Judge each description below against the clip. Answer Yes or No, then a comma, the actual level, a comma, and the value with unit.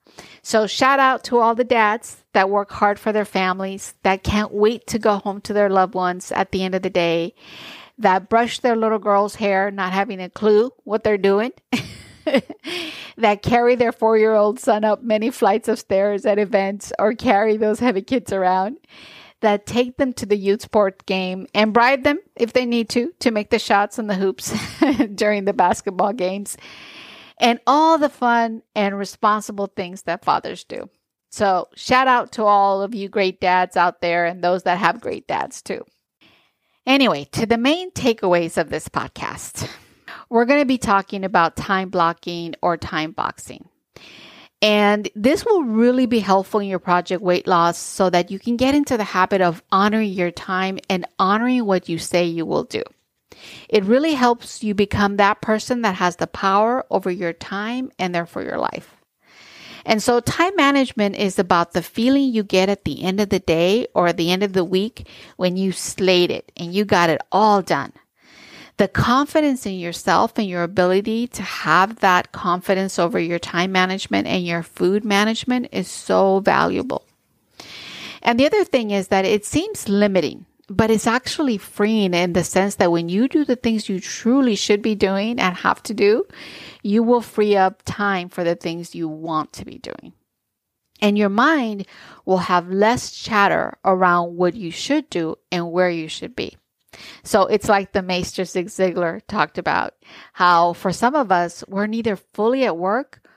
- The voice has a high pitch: Yes, high, 205 Hz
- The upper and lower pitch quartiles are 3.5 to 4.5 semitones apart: Yes, average, 4.0 semitones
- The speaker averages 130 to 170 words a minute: No, average, 185 wpm